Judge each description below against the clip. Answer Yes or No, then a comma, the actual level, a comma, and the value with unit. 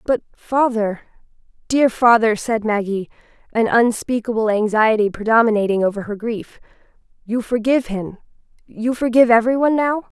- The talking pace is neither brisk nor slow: No, slow, 120 wpm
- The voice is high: Yes, high, 230 Hz